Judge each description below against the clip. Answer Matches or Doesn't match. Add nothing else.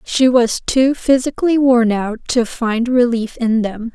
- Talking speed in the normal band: Matches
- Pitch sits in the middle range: Doesn't match